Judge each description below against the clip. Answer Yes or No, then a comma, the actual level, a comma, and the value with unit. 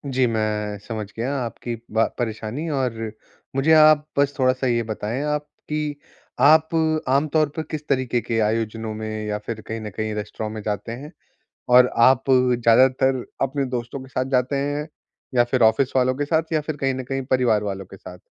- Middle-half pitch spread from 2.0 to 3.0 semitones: No, average, 3.9 semitones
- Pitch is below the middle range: Yes, low, 125 Hz